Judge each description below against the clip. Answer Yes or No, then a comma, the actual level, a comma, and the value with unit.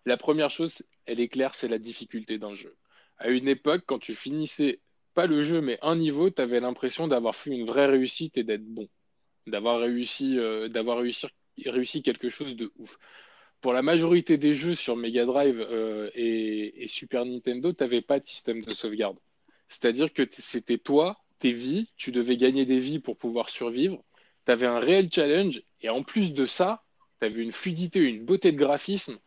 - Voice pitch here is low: Yes, low, 130 Hz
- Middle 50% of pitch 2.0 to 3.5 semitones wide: No, average, 4.3 semitones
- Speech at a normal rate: Yes, average, 195 wpm